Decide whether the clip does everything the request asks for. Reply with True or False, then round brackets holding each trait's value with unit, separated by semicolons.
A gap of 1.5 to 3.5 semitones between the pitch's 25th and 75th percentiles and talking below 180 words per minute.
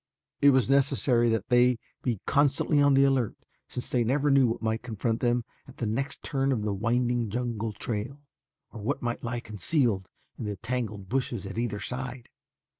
False (3.0 semitones; 185 wpm)